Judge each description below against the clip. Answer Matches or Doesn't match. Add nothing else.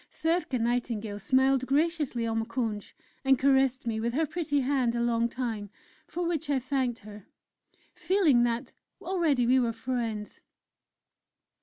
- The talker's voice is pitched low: Doesn't match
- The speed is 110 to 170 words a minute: Matches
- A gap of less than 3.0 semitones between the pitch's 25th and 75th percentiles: Doesn't match